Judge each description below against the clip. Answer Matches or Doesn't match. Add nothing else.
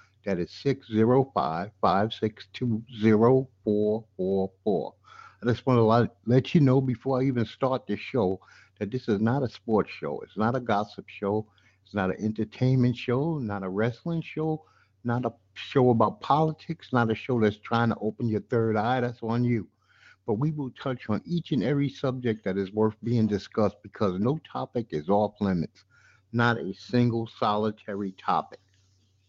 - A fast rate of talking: Doesn't match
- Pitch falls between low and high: Doesn't match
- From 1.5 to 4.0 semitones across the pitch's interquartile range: Matches